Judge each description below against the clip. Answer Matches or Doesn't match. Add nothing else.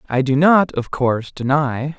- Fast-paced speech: Doesn't match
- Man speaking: Matches